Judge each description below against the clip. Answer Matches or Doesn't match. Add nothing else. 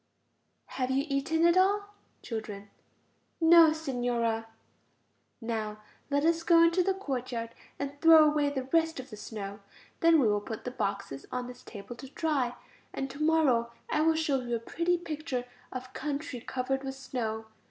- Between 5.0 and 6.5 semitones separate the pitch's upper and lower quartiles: Matches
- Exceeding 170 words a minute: Doesn't match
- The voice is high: Matches